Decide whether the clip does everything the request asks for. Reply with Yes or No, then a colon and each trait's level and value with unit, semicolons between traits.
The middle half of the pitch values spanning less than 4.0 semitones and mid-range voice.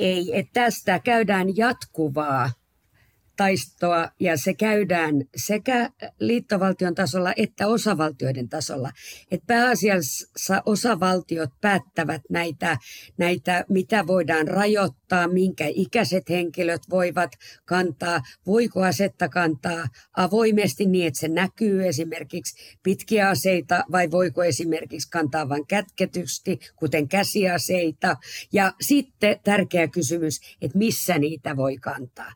Yes: average, 3.6 semitones; medium, 180 Hz